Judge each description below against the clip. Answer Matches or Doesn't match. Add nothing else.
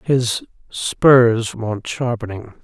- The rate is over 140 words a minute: Doesn't match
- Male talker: Matches